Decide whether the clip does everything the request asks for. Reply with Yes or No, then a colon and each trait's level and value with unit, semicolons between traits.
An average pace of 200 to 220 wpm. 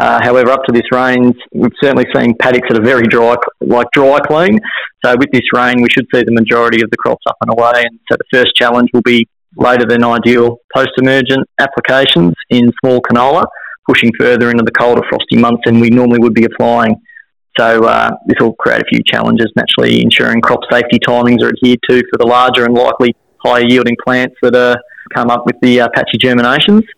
Yes: fast, 205 wpm